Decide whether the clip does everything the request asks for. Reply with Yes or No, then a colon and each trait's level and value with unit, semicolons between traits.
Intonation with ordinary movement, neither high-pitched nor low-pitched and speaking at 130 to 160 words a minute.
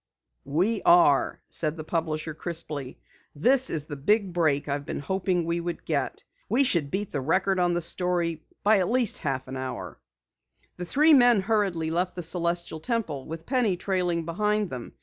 No: average, 4.1 semitones; medium, 175 Hz; average, 175 wpm